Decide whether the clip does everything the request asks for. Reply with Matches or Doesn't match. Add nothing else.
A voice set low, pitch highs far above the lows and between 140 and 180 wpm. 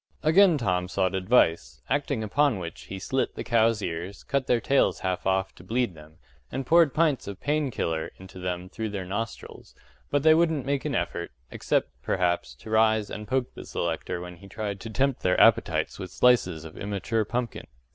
Doesn't match